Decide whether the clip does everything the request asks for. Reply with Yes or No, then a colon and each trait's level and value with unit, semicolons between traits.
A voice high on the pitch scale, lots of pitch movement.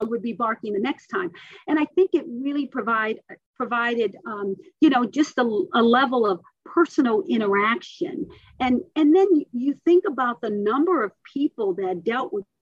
Yes: very high, 275 Hz; wide, 6.7 semitones